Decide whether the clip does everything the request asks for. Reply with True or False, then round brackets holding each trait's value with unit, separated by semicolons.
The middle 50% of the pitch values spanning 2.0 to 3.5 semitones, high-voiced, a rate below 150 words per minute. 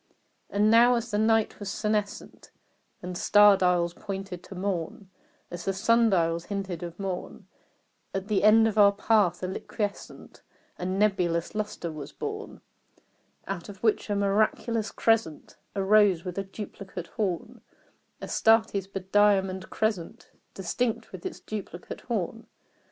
True (2.8 semitones; 200 Hz; 135 wpm)